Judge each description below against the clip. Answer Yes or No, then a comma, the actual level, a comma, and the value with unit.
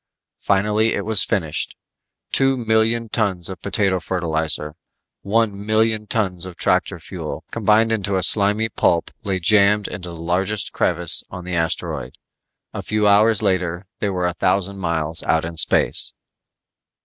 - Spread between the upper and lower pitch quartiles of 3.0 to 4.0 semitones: Yes, average, 3.4 semitones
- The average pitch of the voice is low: Yes, low, 100 Hz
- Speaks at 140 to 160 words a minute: Yes, average, 150 wpm